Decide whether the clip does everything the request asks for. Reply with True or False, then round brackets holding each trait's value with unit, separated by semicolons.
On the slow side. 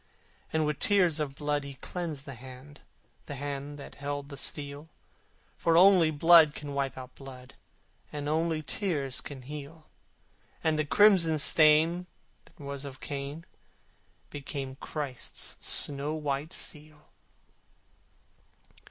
True (125 wpm)